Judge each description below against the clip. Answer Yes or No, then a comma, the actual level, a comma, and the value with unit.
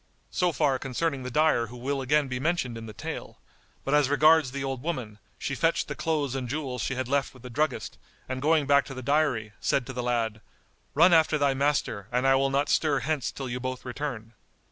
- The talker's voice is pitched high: No, low, 135 Hz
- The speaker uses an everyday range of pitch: Yes, average, 3.0 semitones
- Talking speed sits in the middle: No, fast, 225 wpm